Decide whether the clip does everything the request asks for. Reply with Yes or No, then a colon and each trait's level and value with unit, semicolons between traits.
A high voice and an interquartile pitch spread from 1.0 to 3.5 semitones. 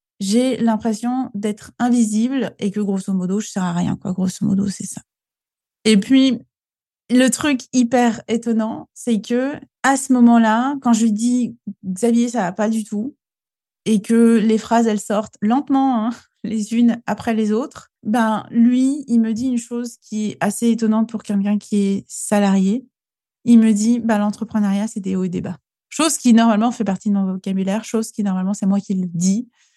Yes: high, 220 Hz; narrow, 2.5 semitones